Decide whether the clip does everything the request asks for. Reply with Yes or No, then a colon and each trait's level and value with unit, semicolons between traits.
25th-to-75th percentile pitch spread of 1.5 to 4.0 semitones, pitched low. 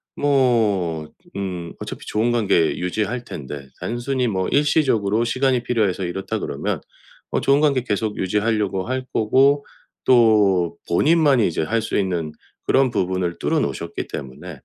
No: wide, 5.6 semitones; low, 110 Hz